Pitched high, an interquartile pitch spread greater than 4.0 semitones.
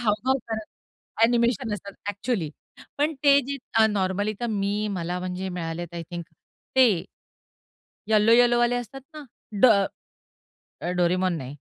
Yes: high, 210 Hz; average, 4.7 semitones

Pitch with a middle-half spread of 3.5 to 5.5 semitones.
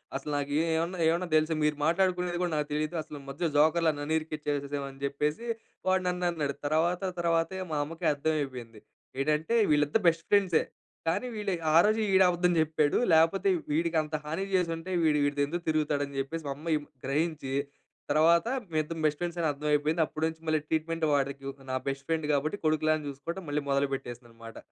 No: average, 2.7 semitones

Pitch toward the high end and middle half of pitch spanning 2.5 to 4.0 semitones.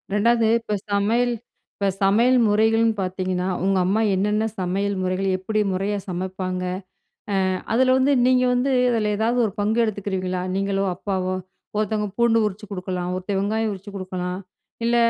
Yes: high, 200 Hz; average, 3.0 semitones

